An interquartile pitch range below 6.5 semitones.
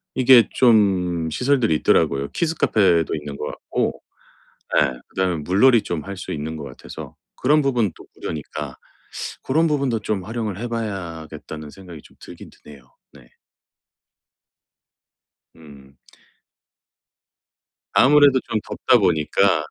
No: wide, 7.5 semitones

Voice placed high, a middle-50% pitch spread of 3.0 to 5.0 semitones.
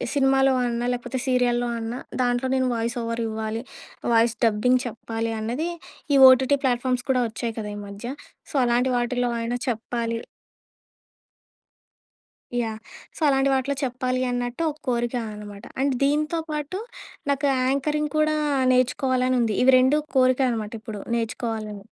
No: high, 245 Hz; narrow, 2.4 semitones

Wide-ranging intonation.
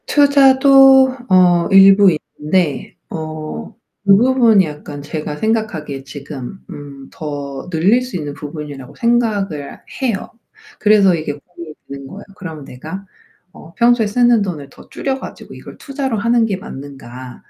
Yes: wide, 7.6 semitones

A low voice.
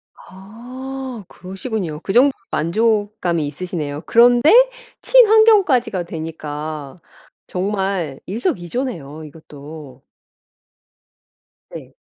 No: high, 190 Hz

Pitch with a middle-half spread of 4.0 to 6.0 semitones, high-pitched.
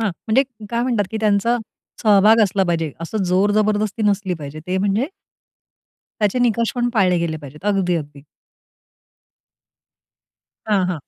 No: average, 3.5 semitones; high, 200 Hz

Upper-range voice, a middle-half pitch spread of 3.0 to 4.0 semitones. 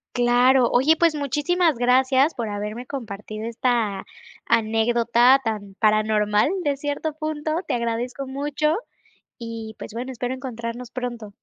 Yes: high, 245 Hz; average, 3.6 semitones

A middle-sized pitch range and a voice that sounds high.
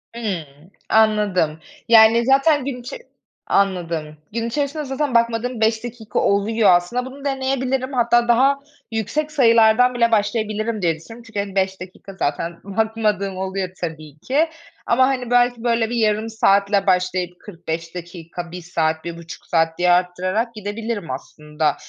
Yes: average, 5.0 semitones; high, 215 Hz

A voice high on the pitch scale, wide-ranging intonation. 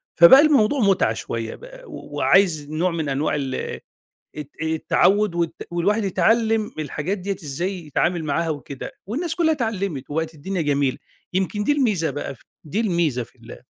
No: medium, 175 Hz; wide, 6.1 semitones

